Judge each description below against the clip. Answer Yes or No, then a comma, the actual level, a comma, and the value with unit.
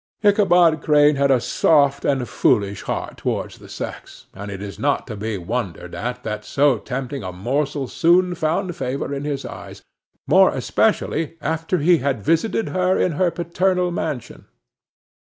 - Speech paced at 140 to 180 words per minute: Yes, average, 160 wpm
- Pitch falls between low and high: Yes, medium, 145 Hz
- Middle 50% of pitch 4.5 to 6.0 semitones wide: Yes, wide, 5.6 semitones